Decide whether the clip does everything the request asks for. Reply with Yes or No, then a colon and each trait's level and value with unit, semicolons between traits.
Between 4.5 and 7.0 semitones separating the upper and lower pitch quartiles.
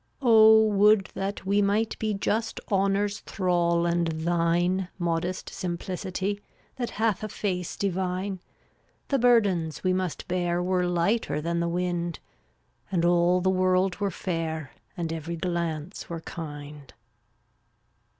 No: average, 2.8 semitones